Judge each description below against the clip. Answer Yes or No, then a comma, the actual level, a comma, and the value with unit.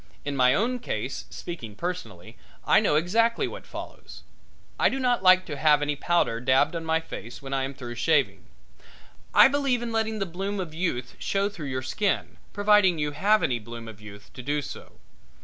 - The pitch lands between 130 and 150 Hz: No, medium, 160 Hz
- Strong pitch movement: Yes, wide, 7.7 semitones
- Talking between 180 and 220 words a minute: Yes, average, 195 wpm